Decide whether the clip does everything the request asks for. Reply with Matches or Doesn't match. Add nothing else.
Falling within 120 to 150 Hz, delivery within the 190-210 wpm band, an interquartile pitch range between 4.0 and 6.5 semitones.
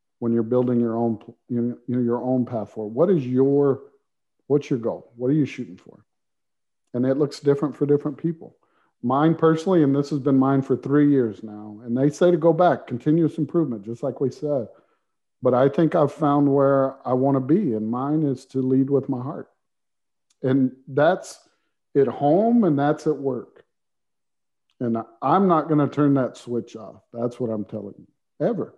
Doesn't match